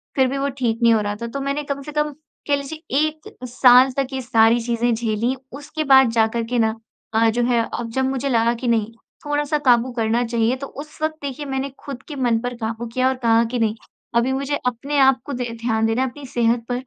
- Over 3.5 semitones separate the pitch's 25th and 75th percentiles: No, average, 3.2 semitones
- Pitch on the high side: Yes, very high, 250 Hz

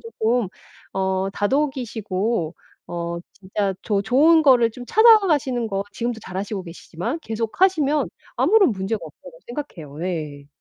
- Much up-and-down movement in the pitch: Yes, wide, 6.3 semitones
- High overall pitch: Yes, high, 220 Hz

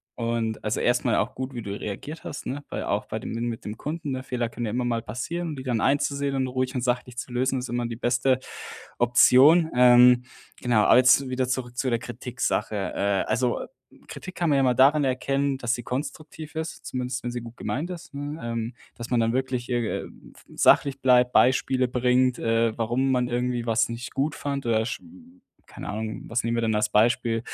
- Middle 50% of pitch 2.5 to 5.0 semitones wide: No, narrow, 2.1 semitones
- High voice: No, low, 125 Hz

